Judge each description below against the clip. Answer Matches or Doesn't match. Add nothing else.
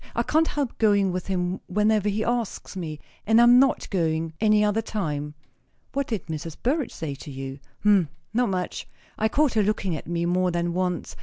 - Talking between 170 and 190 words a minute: Doesn't match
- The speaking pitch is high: Matches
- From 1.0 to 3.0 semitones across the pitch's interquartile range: Doesn't match